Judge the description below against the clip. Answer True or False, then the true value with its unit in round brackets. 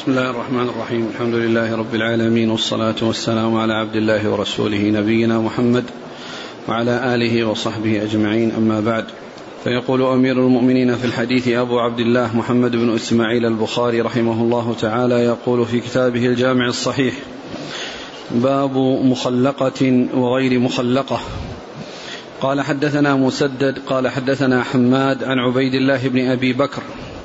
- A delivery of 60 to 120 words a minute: False (130 wpm)